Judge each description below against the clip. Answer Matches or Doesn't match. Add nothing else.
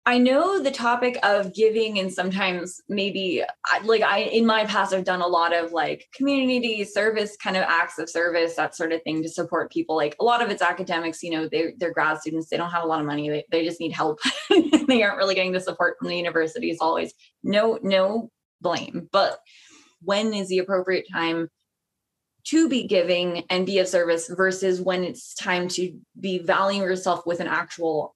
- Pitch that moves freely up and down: Doesn't match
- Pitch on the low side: Doesn't match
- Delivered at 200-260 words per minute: Matches